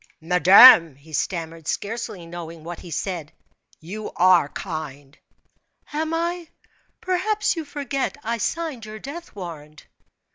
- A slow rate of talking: Yes, slow, 120 wpm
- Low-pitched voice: No, medium, 185 Hz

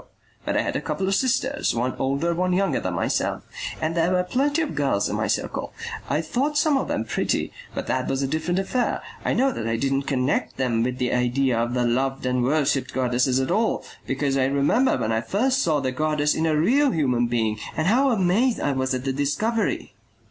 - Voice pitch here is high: No, medium, 145 Hz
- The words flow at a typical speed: No, fast, 220 wpm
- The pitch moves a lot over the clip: Yes, wide, 7.2 semitones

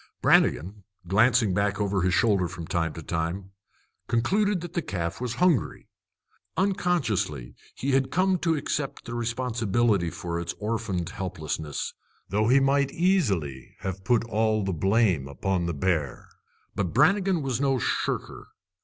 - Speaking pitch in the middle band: No, low, 105 Hz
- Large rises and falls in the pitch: Yes, wide, 7.0 semitones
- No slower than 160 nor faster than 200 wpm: No, average, 145 wpm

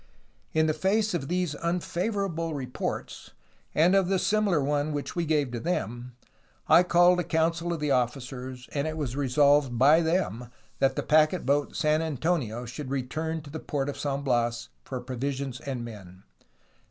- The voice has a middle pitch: Yes, medium, 145 Hz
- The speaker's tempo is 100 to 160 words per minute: No, average, 170 wpm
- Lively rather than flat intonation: No, average, 4.5 semitones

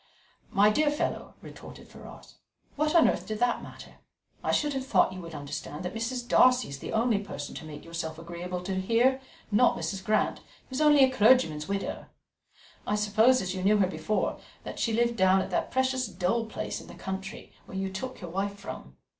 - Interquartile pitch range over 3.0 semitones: Yes, wide, 5.5 semitones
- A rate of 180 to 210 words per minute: Yes, average, 200 wpm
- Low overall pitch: No, high, 205 Hz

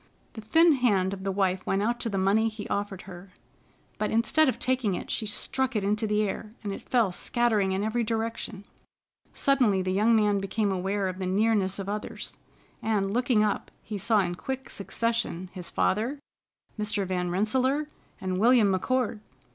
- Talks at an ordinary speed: Yes, average, 180 wpm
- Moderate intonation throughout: Yes, average, 3.1 semitones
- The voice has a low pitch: No, high, 210 Hz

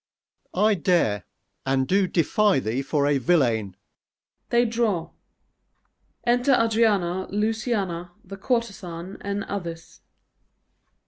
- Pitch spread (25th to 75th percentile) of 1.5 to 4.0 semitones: No, average, 4.8 semitones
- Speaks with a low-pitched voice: No, high, 190 Hz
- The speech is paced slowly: Yes, slow, 105 wpm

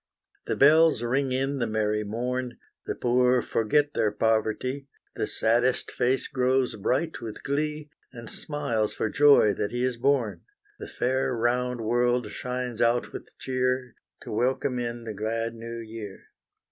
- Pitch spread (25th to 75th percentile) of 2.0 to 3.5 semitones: Yes, narrow, 2.4 semitones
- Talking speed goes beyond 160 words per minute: No, average, 150 wpm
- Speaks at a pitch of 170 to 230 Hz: No, low, 125 Hz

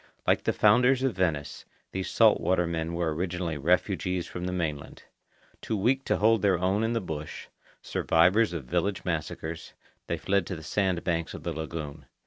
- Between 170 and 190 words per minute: Yes, average, 180 wpm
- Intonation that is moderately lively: Yes, average, 3.4 semitones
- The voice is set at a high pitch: No, very low, 90 Hz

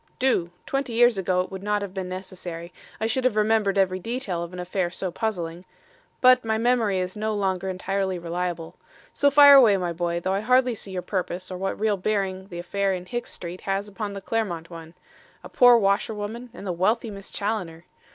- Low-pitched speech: No, high, 195 Hz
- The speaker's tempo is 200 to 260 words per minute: Yes, fast, 205 wpm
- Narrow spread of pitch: No, average, 3.4 semitones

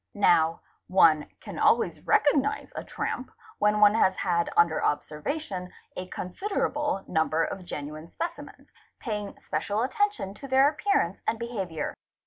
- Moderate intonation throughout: No, wide, 8.6 semitones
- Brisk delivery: No, slow, 135 wpm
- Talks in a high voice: Yes, high, 200 Hz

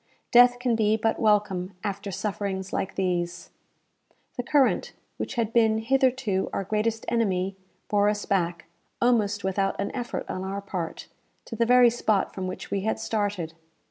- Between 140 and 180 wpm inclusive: Yes, average, 160 wpm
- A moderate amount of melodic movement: Yes, average, 3.2 semitones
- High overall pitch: Yes, high, 205 Hz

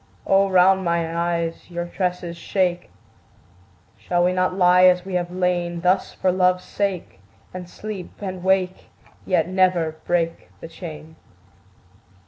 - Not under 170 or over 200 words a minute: No, slow, 135 wpm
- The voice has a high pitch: No, medium, 180 Hz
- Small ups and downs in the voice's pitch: Yes, narrow, 1.3 semitones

